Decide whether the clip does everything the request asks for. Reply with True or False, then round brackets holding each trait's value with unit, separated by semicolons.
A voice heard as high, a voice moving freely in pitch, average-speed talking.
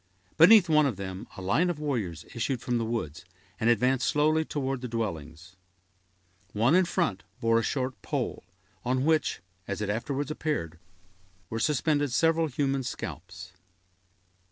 False (125 Hz; 6.7 semitones; 150 wpm)